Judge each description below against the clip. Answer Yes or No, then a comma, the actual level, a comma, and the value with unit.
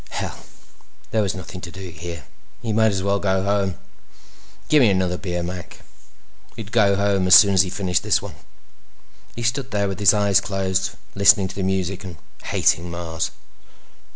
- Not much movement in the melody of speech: Yes, narrow, 1.8 semitones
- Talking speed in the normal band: Yes, average, 175 wpm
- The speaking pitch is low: Yes, very low, 95 Hz